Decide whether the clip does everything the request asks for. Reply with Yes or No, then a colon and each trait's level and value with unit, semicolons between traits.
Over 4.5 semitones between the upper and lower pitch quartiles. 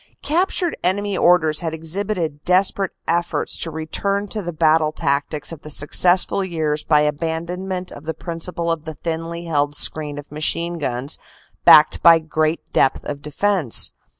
No: average, 2.9 semitones